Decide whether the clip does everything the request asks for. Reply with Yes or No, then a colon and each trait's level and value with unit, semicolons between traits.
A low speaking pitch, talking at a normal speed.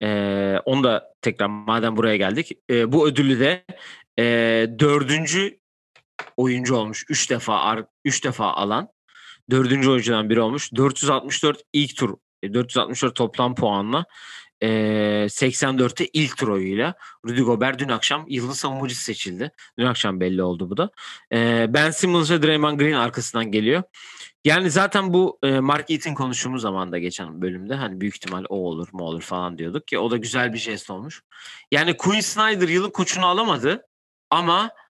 No: low, 125 Hz; fast, 150 wpm